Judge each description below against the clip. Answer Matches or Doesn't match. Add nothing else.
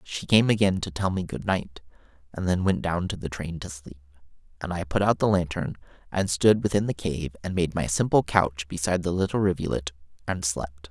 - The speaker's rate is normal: Doesn't match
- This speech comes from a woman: Doesn't match